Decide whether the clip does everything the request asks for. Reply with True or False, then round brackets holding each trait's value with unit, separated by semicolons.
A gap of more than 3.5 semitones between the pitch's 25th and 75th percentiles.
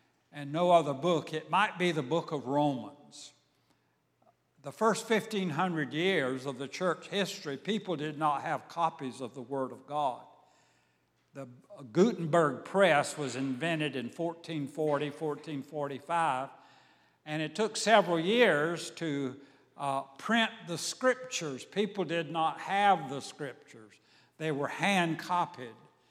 True (4.2 semitones)